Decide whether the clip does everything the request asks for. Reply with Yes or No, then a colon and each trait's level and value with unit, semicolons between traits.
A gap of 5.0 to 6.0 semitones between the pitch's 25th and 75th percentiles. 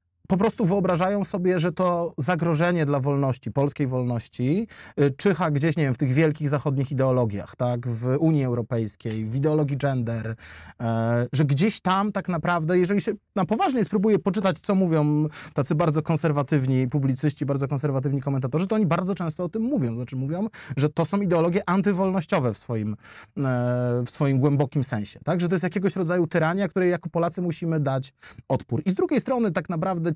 Yes: wide, 5.5 semitones